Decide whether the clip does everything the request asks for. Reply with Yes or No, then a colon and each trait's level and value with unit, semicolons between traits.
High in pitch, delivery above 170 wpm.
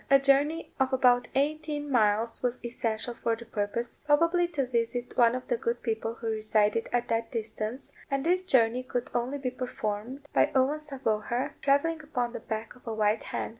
Yes: high, 245 Hz; average, 190 wpm